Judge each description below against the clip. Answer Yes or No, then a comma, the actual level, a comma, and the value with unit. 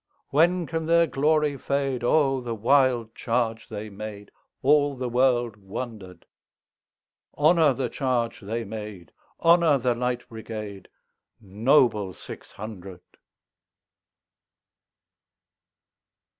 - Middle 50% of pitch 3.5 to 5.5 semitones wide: Yes, average, 4.7 semitones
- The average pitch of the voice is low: Yes, low, 120 Hz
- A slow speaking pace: Yes, slow, 80 wpm